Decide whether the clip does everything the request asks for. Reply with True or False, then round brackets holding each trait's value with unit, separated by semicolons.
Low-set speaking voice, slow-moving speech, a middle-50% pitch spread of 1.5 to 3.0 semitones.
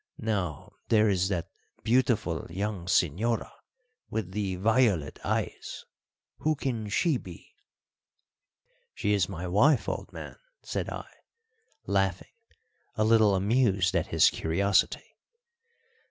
False (100 Hz; 110 wpm; 3.5 semitones)